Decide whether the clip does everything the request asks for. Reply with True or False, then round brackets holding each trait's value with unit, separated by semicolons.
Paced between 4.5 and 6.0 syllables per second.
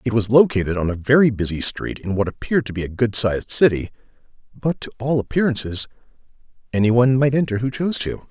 False (6.5 syllables/s)